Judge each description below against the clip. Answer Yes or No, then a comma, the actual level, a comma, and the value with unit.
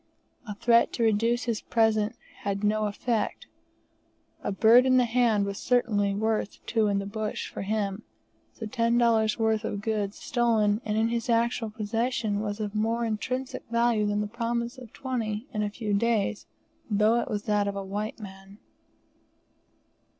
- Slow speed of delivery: No, average, 170 wpm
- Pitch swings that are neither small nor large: No, narrow, 2.1 semitones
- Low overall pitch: No, high, 220 Hz